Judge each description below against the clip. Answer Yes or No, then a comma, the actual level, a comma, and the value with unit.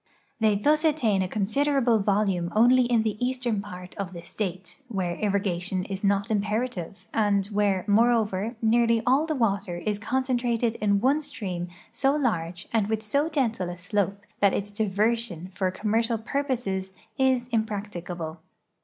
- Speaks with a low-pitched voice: No, high, 210 Hz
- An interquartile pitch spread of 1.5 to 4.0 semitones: Yes, average, 3.7 semitones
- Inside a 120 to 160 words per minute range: Yes, average, 155 wpm